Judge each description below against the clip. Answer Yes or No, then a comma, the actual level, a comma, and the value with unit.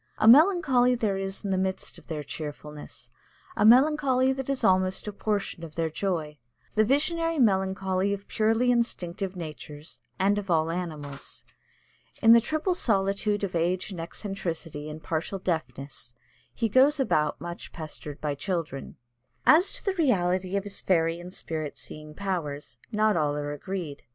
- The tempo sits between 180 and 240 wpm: No, average, 160 wpm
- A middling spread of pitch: No, wide, 5.7 semitones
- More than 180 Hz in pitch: Yes, high, 190 Hz